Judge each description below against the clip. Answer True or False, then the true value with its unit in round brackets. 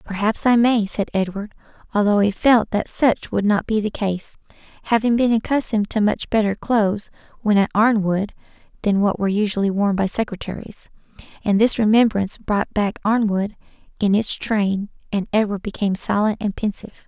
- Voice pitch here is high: True (210 Hz)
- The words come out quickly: False (165 wpm)